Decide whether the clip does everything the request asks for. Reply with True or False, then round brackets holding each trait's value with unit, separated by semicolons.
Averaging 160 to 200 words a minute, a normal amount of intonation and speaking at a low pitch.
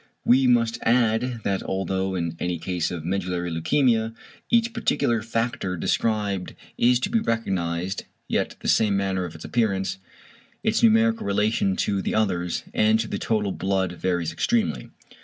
False (150 wpm; 4.1 semitones; 100 Hz)